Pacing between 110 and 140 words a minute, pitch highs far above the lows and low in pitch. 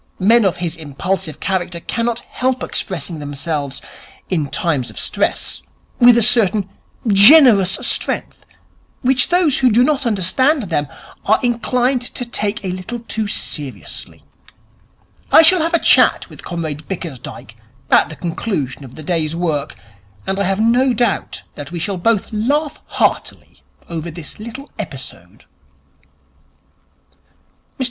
No: slow, 135 wpm; wide, 6.7 semitones; high, 195 Hz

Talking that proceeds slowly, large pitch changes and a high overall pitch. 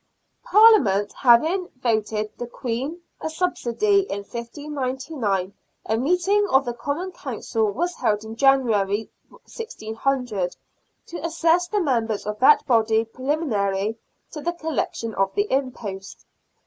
Yes: slow, 120 wpm; wide, 6.8 semitones; very high, 255 Hz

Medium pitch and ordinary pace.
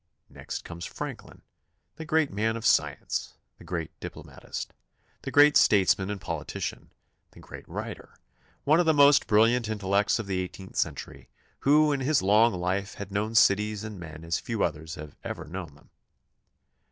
No: low, 100 Hz; average, 165 wpm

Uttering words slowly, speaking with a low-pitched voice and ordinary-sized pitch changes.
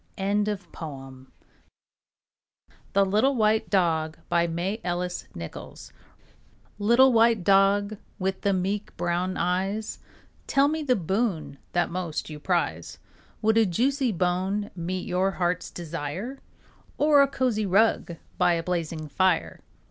No: slow, 110 wpm; high, 190 Hz; average, 3.9 semitones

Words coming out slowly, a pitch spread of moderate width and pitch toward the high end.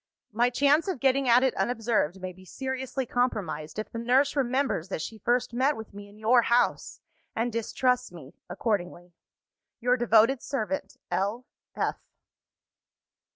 No: average, 145 wpm; average, 3.6 semitones; high, 240 Hz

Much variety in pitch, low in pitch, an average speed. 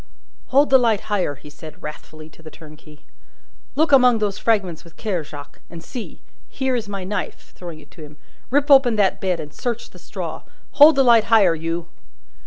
No: wide, 7.2 semitones; high, 195 Hz; average, 190 wpm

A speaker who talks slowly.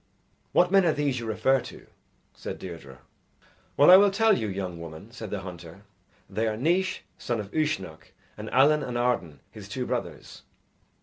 No: average, 175 wpm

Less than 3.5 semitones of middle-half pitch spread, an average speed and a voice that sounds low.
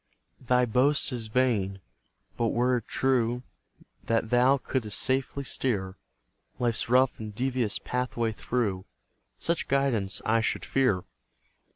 No: average, 2.8 semitones; slow, 120 wpm; low, 120 Hz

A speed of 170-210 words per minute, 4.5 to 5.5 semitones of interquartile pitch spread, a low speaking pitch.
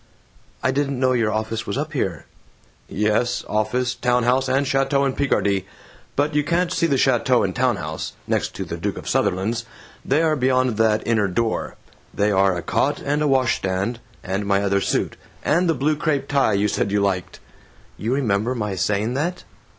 Yes: average, 190 wpm; average, 5.1 semitones; low, 120 Hz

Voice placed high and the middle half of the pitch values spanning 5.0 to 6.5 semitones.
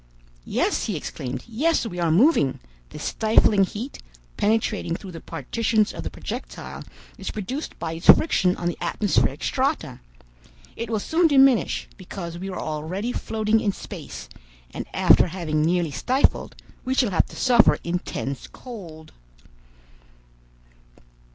Yes: high, 195 Hz; wide, 5.5 semitones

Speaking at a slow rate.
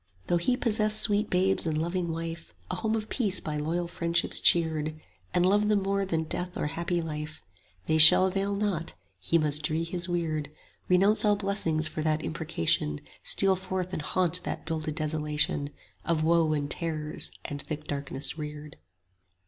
No: average, 175 wpm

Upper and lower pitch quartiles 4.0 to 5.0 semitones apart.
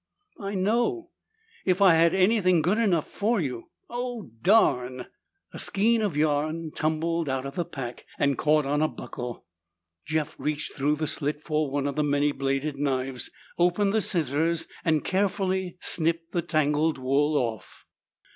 Yes: average, 4.6 semitones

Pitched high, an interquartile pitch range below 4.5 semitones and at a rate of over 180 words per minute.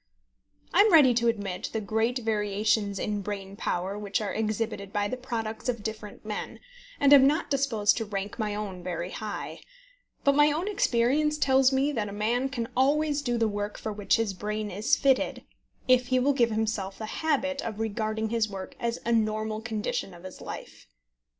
Yes: high, 220 Hz; average, 3.8 semitones; average, 190 wpm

